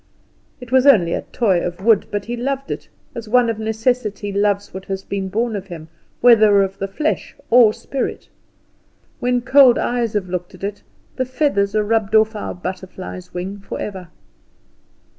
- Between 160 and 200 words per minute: Yes, average, 175 wpm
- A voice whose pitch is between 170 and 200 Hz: No, high, 210 Hz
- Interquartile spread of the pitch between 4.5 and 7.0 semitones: No, average, 3.8 semitones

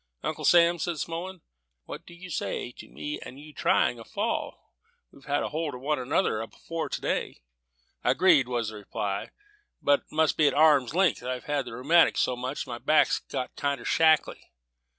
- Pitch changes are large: No, average, 4.5 semitones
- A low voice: No, medium, 145 Hz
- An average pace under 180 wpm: No, average, 190 wpm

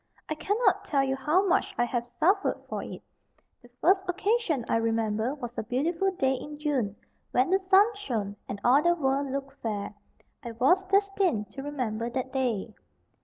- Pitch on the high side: Yes, very high, 270 Hz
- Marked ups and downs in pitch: Yes, wide, 7.1 semitones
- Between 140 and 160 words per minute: No, average, 175 wpm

